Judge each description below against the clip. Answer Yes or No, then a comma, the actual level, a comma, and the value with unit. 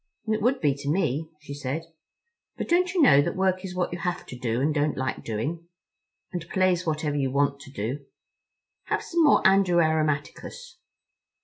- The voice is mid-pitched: Yes, medium, 155 Hz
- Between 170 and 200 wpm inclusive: Yes, average, 185 wpm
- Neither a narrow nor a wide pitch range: Yes, average, 4.8 semitones